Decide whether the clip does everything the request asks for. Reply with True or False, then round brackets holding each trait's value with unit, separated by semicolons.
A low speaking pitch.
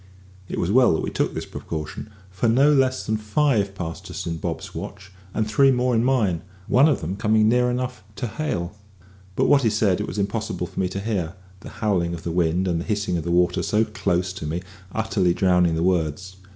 True (100 Hz)